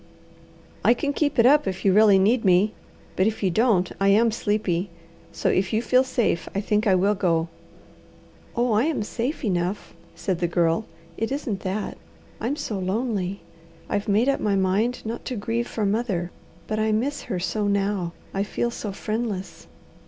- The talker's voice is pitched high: Yes, high, 210 Hz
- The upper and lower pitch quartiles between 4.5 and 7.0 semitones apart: No, average, 3.6 semitones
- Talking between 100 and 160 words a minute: No, average, 180 wpm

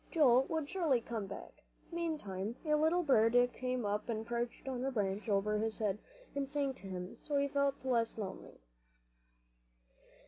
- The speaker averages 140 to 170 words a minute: Yes, average, 165 wpm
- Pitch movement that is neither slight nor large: Yes, average, 4.9 semitones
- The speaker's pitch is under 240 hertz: No, high, 245 Hz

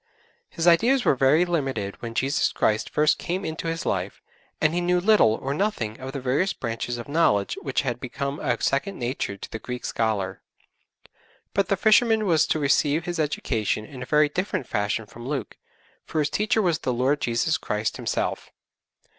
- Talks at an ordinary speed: Yes, average, 185 wpm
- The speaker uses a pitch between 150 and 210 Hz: No, medium, 140 Hz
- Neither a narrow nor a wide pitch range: No, wide, 6.2 semitones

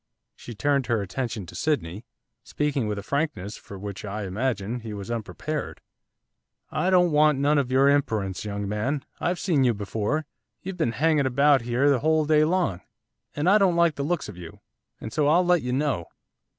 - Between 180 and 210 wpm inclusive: Yes, average, 190 wpm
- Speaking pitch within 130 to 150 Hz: Yes, low, 135 Hz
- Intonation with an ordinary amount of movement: No, wide, 6.3 semitones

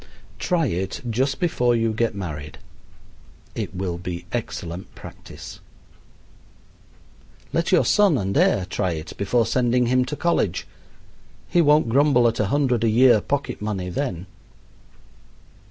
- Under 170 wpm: Yes, slow, 135 wpm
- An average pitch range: No, wide, 6.5 semitones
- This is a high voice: No, low, 115 Hz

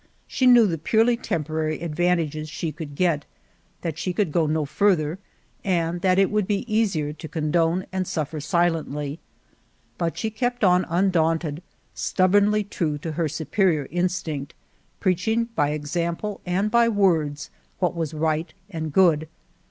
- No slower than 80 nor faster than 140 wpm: No, average, 150 wpm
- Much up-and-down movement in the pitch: No, average, 3.7 semitones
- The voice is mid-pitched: Yes, medium, 170 Hz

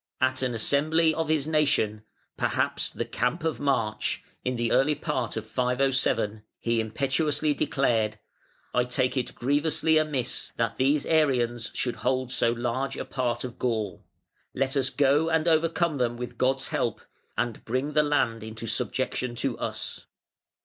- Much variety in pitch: No, average, 3.8 semitones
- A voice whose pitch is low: Yes, low, 130 Hz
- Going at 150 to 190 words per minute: Yes, average, 155 wpm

